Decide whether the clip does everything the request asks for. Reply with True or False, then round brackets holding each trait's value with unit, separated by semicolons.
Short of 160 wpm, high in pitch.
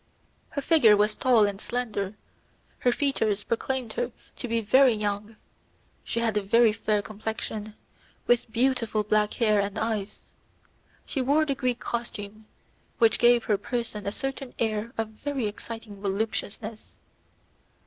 True (140 wpm; 225 Hz)